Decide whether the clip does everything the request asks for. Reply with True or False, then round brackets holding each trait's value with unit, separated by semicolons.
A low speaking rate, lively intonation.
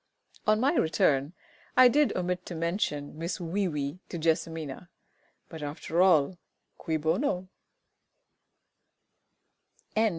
False (105 wpm; 2.9 semitones)